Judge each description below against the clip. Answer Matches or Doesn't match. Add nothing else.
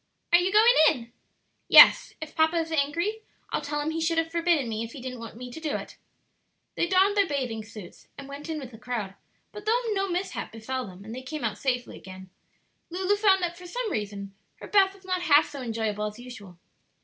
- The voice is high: Matches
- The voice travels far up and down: Matches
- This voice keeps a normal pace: Doesn't match